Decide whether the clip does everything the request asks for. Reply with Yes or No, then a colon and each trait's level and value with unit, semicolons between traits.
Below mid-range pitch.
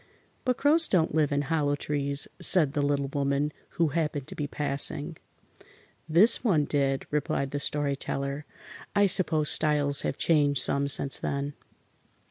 No: medium, 145 Hz